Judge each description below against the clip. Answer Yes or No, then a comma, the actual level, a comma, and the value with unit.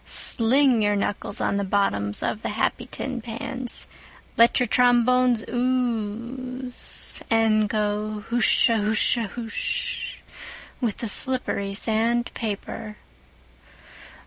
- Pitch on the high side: Yes, high, 225 Hz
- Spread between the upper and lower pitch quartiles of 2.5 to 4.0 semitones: Yes, average, 2.8 semitones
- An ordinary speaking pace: No, slow, 100 wpm